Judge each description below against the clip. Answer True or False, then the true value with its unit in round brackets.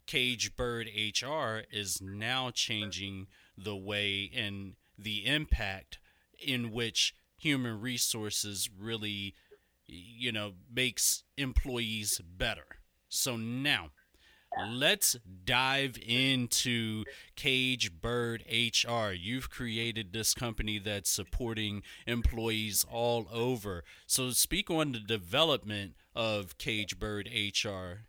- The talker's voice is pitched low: True (115 Hz)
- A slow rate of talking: True (100 wpm)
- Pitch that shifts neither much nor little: True (3.3 semitones)